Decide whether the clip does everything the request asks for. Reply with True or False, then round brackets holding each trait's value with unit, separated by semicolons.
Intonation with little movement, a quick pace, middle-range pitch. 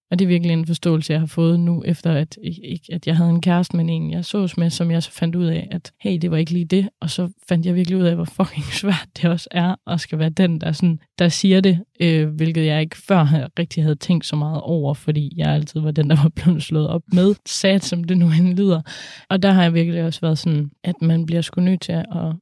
True (1.9 semitones; 270 wpm; 170 Hz)